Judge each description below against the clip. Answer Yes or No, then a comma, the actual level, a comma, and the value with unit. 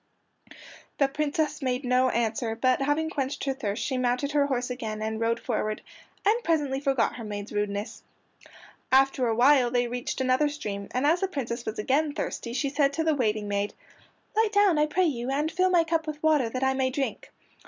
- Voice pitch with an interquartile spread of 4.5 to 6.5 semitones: No, average, 4.1 semitones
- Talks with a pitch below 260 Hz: No, very high, 265 Hz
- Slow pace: No, average, 195 wpm